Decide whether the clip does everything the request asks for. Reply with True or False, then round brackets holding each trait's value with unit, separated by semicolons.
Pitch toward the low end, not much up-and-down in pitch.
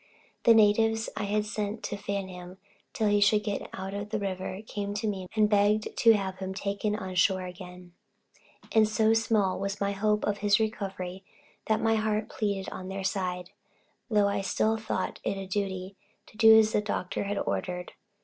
False (205 Hz; 2.0 semitones)